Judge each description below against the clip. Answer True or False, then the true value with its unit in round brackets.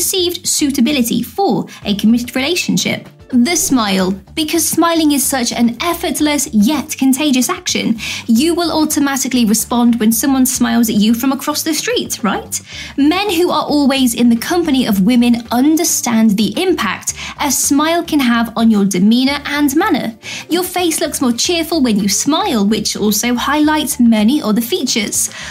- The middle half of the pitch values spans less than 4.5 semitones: False (5.1 semitones)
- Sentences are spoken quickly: False (155 wpm)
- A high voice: True (265 Hz)